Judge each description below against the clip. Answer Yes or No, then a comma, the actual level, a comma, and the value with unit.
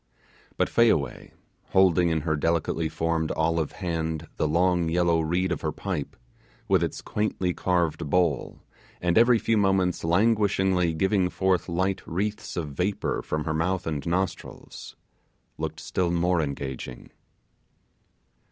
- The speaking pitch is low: Yes, very low, 85 Hz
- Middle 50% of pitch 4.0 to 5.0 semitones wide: No, average, 2.7 semitones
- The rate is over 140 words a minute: No, slow, 135 wpm